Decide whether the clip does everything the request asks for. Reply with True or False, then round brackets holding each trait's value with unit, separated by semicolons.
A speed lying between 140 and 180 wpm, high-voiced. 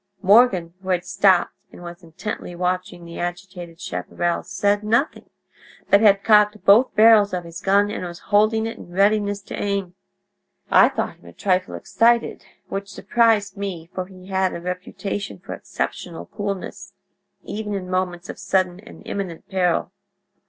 True (160 wpm; 195 Hz)